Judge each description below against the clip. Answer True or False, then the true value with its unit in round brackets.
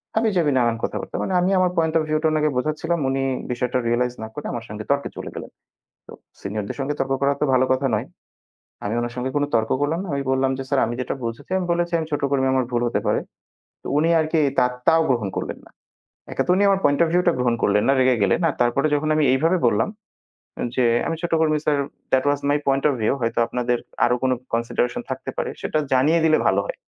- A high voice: False (135 Hz)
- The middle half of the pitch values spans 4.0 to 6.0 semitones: True (4.5 semitones)